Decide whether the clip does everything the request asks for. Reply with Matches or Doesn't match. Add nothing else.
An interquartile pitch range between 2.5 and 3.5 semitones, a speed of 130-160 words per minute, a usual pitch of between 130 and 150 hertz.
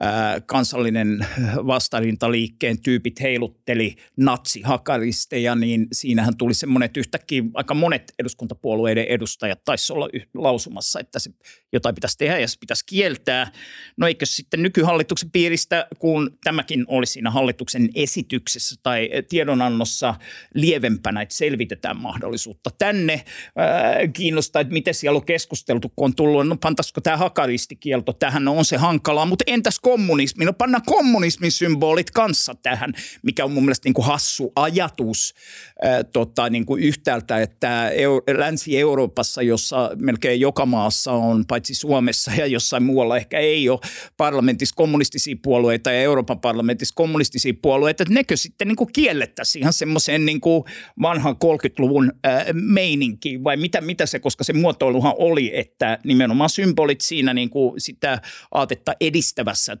Doesn't match